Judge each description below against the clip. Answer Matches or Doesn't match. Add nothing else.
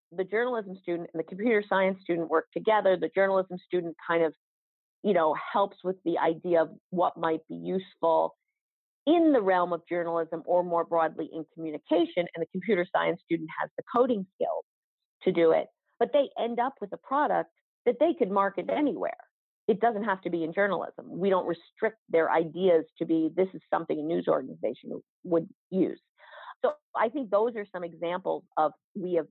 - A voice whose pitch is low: Doesn't match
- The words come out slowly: Doesn't match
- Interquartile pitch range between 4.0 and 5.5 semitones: Doesn't match